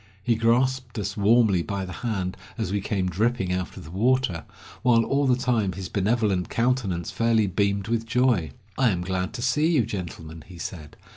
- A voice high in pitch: No, low, 105 Hz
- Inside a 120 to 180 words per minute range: No, average, 190 wpm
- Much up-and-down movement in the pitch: No, average, 4.6 semitones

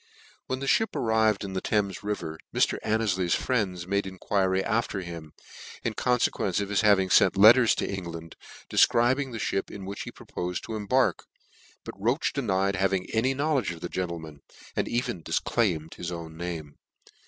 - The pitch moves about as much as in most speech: Yes, average, 4.2 semitones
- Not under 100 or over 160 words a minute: No, average, 170 wpm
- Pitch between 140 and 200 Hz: No, low, 100 Hz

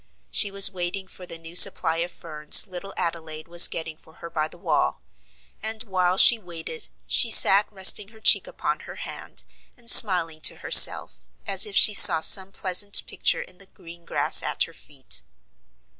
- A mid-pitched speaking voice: Yes, medium, 180 Hz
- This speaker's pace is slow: No, average, 180 wpm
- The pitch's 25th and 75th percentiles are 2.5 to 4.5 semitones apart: Yes, average, 3.3 semitones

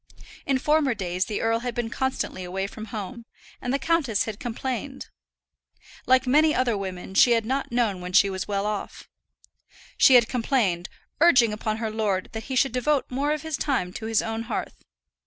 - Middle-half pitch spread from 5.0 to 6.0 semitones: No, average, 4.4 semitones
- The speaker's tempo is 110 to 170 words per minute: No, average, 190 wpm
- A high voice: Yes, high, 230 Hz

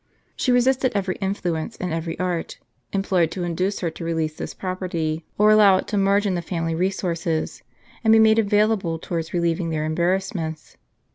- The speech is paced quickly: No, average, 170 wpm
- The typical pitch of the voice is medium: Yes, medium, 180 Hz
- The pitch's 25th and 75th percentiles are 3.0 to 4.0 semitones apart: Yes, average, 3.4 semitones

